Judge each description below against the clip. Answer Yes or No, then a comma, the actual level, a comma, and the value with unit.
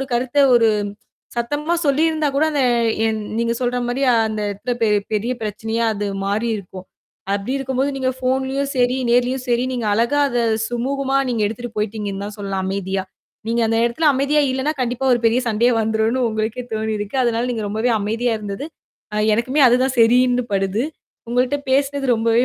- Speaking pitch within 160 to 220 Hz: No, high, 240 Hz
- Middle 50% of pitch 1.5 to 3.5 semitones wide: Yes, average, 3.1 semitones